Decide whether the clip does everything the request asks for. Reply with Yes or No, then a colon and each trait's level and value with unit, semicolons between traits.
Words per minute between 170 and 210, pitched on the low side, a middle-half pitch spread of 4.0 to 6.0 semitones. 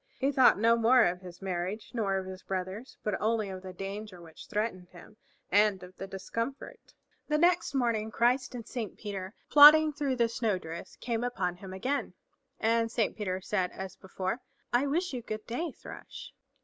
No: average, 185 wpm; high, 215 Hz; average, 4.7 semitones